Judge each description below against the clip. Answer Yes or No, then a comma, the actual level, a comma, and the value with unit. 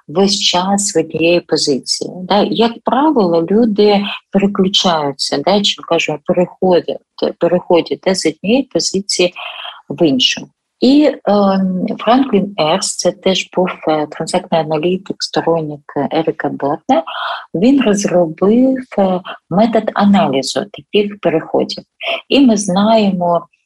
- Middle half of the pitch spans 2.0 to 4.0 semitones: Yes, average, 3.7 semitones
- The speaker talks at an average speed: No, slow, 100 wpm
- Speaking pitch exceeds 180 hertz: Yes, high, 190 Hz